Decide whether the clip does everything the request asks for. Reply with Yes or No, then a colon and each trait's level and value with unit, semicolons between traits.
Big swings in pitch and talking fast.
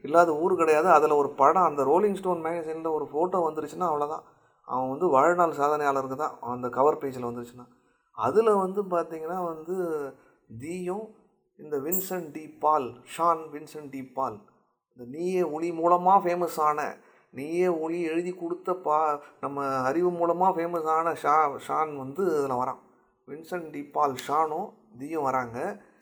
No: average, 3.6 semitones; fast, 135 wpm